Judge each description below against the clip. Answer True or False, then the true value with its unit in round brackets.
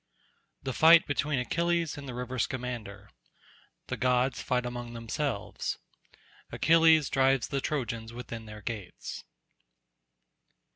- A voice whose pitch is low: True (125 Hz)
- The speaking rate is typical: False (100 wpm)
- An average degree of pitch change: True (3.4 semitones)